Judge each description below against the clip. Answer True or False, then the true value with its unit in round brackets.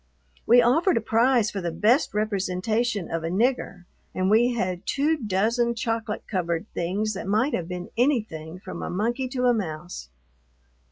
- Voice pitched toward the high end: True (215 Hz)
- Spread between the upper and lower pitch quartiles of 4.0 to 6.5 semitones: True (4.8 semitones)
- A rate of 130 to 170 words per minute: True (165 wpm)